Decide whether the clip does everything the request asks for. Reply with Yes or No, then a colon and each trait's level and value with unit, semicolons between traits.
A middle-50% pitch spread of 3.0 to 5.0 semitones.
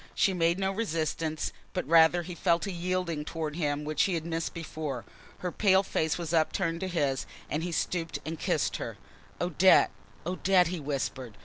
No: narrow, 2.6 semitones